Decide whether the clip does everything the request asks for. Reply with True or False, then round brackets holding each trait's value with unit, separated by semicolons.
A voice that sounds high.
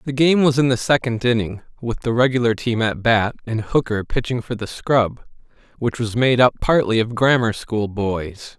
False (120 Hz)